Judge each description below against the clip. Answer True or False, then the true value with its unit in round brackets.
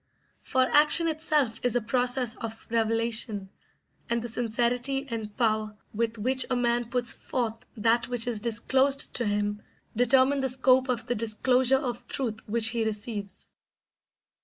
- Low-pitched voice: False (235 Hz)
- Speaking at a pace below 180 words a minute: True (150 wpm)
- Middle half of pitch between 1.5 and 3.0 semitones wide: True (2.4 semitones)